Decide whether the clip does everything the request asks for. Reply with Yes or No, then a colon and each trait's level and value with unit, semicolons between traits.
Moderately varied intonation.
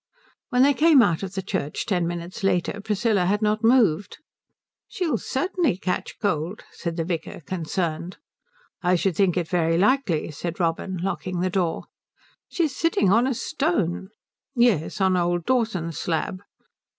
Yes: average, 4.7 semitones